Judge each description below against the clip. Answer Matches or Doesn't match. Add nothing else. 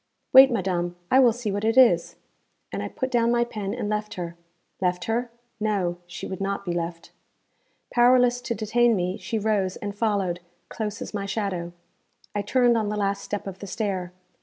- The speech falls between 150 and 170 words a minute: Doesn't match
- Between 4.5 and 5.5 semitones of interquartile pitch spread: Doesn't match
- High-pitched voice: Matches